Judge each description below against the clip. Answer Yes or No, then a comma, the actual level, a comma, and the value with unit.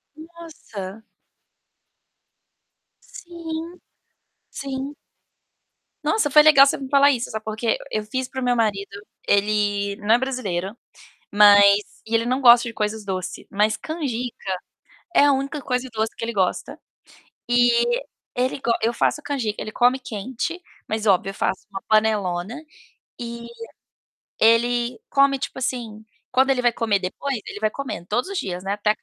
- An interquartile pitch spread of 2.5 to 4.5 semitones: Yes, average, 4.0 semitones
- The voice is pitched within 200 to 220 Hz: No, high, 235 Hz